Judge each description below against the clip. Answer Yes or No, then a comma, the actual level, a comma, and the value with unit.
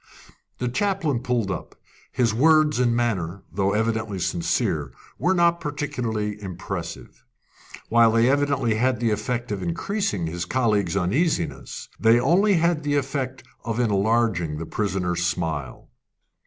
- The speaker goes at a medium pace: No, slow, 130 wpm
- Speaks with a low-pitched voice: Yes, low, 115 Hz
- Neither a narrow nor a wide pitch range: No, wide, 6.1 semitones